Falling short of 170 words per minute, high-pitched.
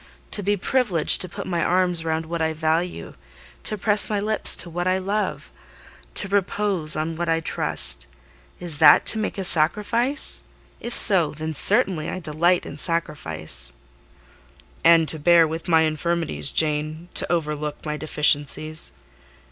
No: average, 150 wpm; medium, 165 Hz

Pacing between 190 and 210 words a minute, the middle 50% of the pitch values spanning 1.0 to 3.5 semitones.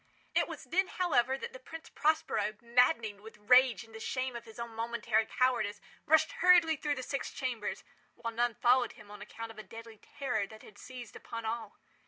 Yes: average, 200 wpm; average, 3.2 semitones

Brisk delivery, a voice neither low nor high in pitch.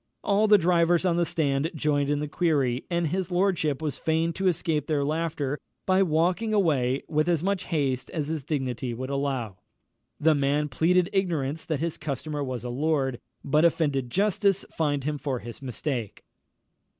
No: average, 175 wpm; medium, 155 Hz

